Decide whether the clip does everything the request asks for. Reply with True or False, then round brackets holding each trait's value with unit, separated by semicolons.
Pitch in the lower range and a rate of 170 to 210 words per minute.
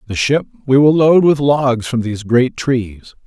True (130 Hz; 200 wpm)